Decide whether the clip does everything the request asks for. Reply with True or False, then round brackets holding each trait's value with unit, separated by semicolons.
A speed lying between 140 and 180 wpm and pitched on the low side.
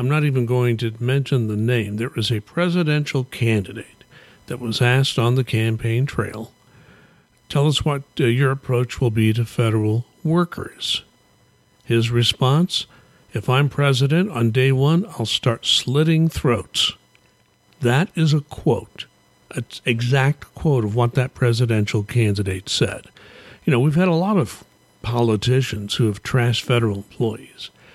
True (150 wpm; 125 Hz)